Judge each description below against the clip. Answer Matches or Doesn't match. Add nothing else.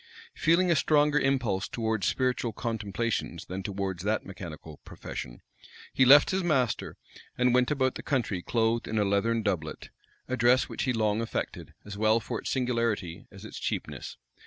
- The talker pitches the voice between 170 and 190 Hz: Doesn't match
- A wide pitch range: Doesn't match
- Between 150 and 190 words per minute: Matches